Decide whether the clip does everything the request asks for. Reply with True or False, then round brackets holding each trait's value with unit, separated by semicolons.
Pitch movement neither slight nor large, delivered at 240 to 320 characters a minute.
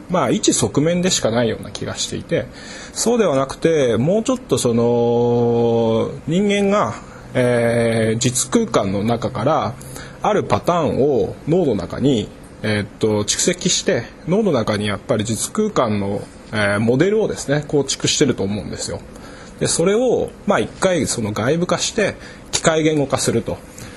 False (7.2 semitones; 285 characters per minute)